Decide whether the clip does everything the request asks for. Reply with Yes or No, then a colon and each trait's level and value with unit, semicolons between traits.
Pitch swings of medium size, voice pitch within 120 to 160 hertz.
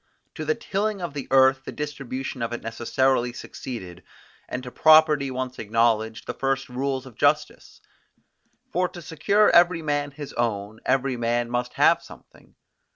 Yes: average, 3.8 semitones; low, 135 Hz